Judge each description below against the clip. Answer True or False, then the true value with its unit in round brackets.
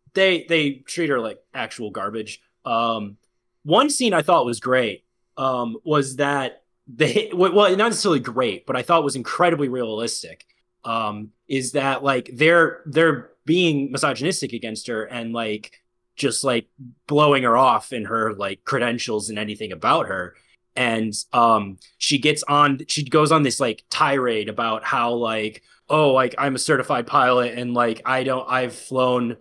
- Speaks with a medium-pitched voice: False (130 Hz)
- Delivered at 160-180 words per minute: True (165 wpm)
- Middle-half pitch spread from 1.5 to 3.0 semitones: False (4.2 semitones)